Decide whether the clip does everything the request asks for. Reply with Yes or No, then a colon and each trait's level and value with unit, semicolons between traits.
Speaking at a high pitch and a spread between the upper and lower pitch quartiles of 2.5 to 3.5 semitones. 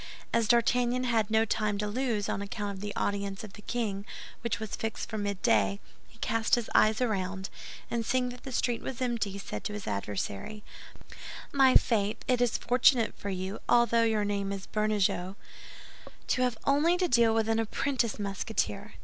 Yes: high, 220 Hz; average, 3.0 semitones